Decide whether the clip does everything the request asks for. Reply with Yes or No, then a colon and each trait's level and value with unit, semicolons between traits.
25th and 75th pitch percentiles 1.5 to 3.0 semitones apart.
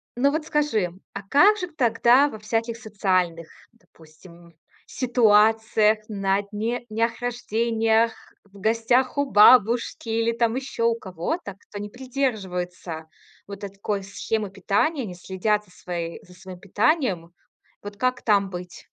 No: average, 3.8 semitones